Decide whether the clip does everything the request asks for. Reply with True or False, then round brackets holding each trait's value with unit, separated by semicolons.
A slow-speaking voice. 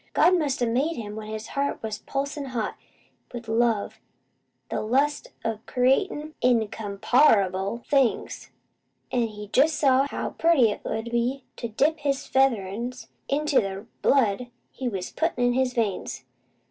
False (160 wpm)